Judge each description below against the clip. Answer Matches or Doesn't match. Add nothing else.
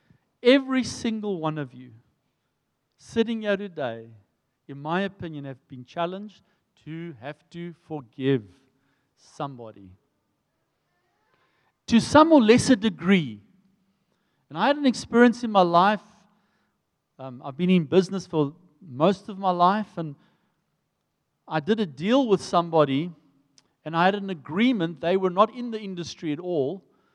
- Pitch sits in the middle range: Matches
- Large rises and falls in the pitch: Matches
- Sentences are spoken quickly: Doesn't match